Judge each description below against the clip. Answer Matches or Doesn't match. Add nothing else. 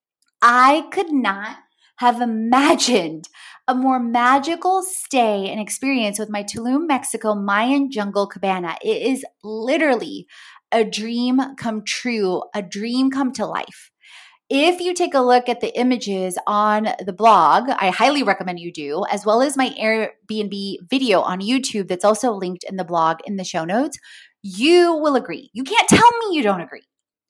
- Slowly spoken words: Doesn't match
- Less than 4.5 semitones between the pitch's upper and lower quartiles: Doesn't match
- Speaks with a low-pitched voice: Doesn't match